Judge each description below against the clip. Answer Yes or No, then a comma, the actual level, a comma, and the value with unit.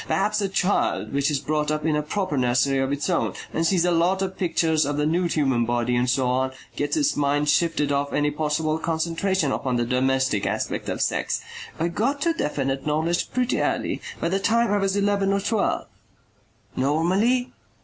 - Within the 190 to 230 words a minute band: Yes, average, 195 wpm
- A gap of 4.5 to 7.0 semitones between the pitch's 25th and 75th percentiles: Yes, wide, 5.5 semitones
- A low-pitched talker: No, medium, 155 Hz